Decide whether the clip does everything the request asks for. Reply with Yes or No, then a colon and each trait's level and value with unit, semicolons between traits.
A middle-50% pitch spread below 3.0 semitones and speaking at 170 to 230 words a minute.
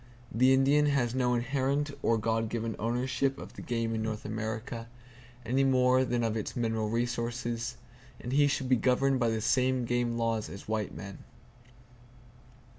No: narrow, 2.4 semitones; average, 160 wpm